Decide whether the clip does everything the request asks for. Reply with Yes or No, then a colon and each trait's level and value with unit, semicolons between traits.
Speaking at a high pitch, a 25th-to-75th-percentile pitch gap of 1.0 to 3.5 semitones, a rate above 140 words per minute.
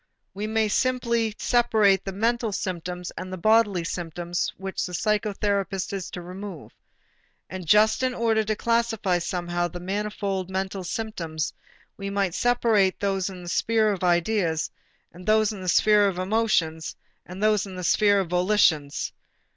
Yes: high, 195 Hz; average, 3.2 semitones; average, 150 wpm